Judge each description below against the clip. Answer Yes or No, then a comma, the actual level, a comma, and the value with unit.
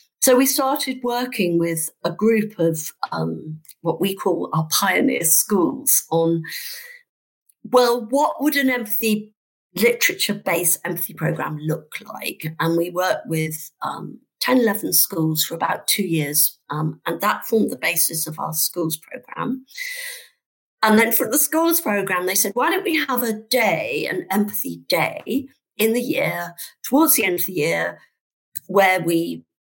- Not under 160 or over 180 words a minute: No, average, 150 wpm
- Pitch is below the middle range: No, high, 200 Hz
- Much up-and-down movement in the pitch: Yes, wide, 7.4 semitones